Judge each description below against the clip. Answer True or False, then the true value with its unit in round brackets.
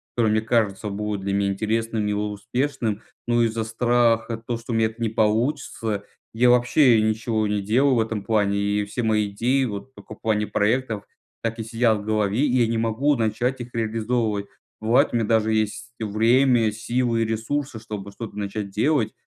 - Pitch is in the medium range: False (110 Hz)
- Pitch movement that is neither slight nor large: False (2.1 semitones)